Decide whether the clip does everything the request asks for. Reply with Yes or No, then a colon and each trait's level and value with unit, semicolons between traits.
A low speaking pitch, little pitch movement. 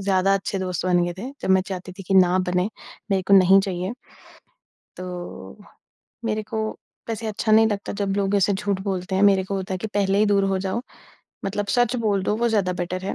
No: high, 195 Hz; narrow, 1.8 semitones